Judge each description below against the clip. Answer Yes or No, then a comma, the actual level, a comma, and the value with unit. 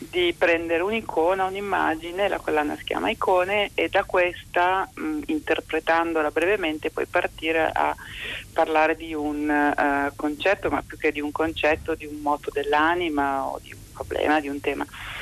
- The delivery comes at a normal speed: Yes, average, 160 wpm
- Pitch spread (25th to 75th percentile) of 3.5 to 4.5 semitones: Yes, average, 3.8 semitones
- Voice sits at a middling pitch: Yes, medium, 160 Hz